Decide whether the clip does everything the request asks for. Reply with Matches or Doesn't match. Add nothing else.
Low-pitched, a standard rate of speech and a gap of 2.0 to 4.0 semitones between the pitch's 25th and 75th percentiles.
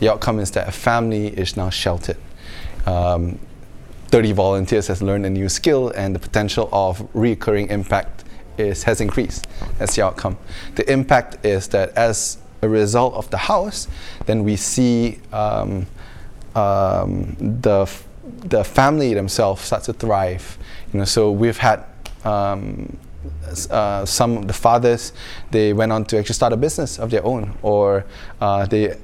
Doesn't match